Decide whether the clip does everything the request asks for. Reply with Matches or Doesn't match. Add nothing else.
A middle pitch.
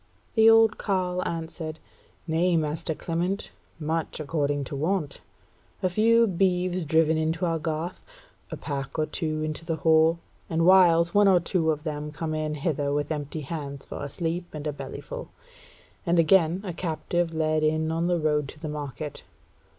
Matches